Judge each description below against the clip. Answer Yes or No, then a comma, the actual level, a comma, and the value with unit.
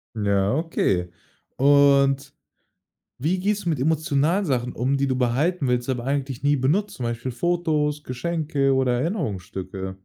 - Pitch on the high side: No, medium, 140 Hz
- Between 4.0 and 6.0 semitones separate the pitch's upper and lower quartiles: Yes, average, 4.4 semitones